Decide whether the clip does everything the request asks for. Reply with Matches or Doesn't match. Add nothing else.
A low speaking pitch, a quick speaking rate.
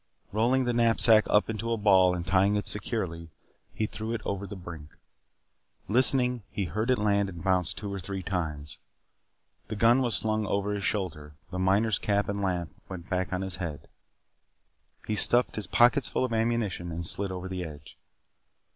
Doesn't match